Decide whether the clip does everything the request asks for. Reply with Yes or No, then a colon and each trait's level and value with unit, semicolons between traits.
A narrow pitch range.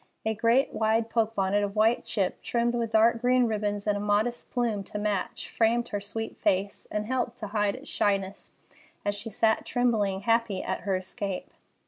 Yes: narrow, 2.3 semitones